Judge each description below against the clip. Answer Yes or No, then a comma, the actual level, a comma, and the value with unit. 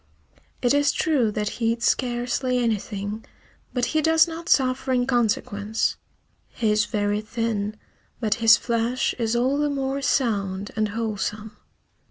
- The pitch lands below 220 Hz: No, high, 230 Hz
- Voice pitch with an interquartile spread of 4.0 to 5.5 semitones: No, average, 3.3 semitones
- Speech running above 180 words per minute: No, average, 145 wpm